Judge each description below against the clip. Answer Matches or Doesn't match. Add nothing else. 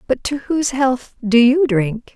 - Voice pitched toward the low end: Doesn't match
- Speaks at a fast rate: Doesn't match